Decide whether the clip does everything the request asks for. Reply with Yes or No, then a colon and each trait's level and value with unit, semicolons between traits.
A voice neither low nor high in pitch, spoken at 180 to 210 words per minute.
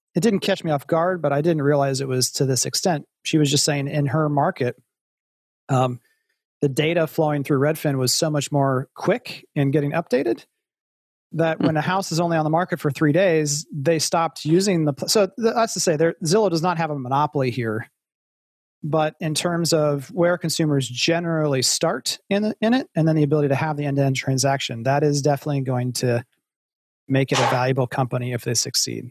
Yes: medium, 150 Hz; fast, 205 wpm